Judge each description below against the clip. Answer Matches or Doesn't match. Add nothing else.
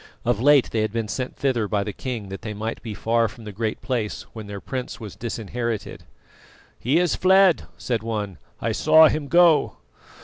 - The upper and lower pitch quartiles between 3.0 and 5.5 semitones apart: Matches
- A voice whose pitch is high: Doesn't match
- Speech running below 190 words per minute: Doesn't match